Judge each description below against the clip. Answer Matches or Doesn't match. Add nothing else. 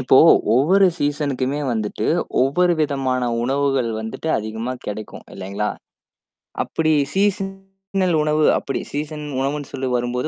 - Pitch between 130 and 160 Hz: Matches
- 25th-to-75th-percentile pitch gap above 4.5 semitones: Doesn't match